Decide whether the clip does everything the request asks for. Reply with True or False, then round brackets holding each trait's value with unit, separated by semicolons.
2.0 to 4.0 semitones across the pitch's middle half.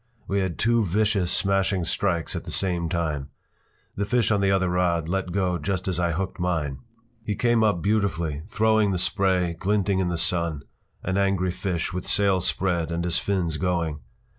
True (2.6 semitones)